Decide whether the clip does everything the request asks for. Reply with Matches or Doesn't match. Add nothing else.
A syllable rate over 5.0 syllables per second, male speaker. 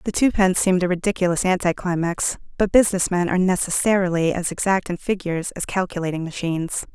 Doesn't match